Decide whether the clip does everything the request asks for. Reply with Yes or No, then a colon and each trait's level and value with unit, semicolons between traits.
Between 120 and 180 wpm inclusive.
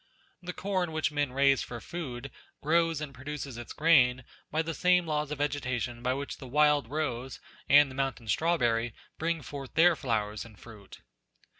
Yes: average, 170 wpm